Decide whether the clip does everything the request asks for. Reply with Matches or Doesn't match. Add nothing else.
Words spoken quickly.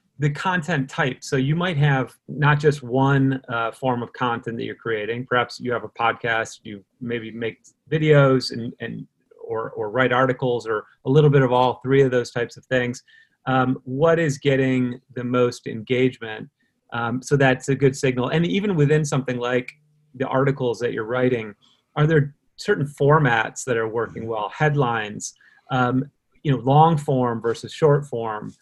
Doesn't match